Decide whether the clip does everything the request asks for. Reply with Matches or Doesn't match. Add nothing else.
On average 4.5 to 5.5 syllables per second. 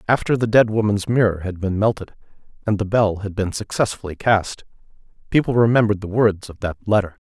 Doesn't match